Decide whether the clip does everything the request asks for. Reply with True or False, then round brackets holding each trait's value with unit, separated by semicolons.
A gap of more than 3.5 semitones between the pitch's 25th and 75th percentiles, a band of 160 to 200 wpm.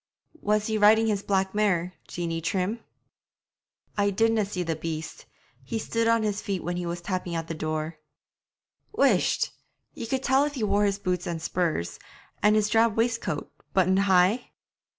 True (4.0 semitones; 170 wpm)